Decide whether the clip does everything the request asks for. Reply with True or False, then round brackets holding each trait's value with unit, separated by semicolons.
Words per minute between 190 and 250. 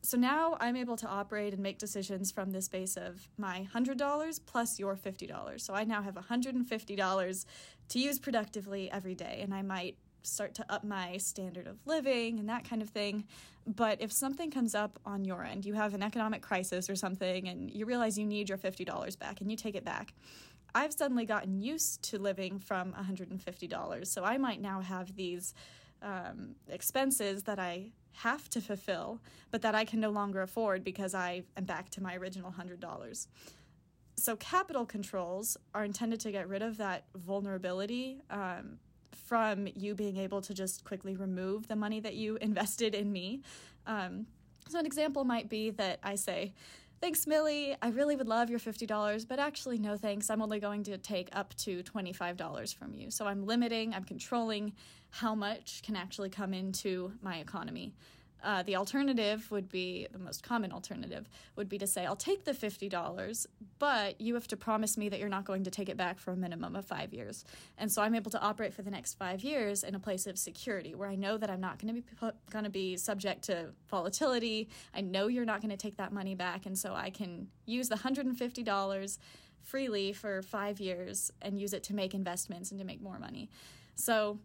True (205 wpm)